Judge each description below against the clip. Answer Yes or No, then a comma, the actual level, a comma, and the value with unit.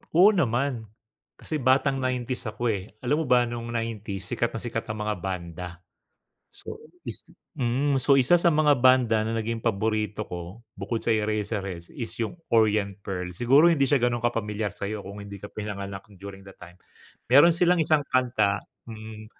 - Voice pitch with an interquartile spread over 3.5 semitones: Yes, average, 4.1 semitones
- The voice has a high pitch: No, low, 115 Hz